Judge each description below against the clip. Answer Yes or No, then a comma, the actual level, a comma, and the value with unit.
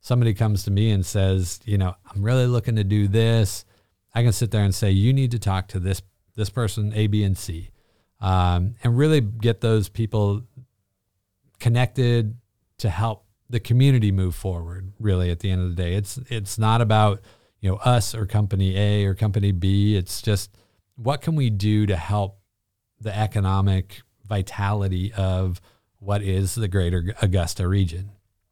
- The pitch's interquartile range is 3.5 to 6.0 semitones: No, average, 2.7 semitones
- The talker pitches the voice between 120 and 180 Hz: No, low, 105 Hz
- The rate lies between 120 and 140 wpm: No, average, 175 wpm